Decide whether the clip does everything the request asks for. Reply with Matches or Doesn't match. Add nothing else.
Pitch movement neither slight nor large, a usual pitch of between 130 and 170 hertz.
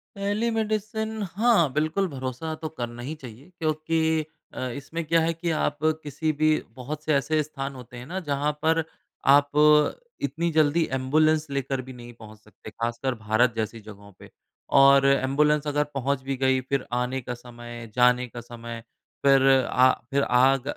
Matches